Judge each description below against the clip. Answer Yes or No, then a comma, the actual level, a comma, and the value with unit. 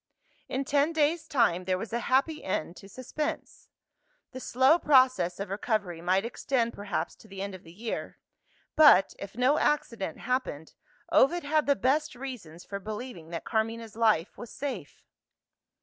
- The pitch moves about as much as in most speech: No, wide, 5.9 semitones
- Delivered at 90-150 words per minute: No, average, 160 wpm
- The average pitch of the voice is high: Yes, high, 230 Hz